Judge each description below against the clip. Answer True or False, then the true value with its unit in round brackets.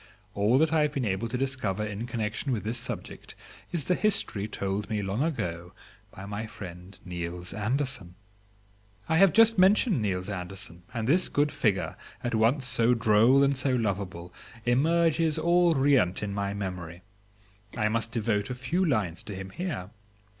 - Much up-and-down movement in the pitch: True (6.1 semitones)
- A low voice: True (110 Hz)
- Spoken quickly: False (170 wpm)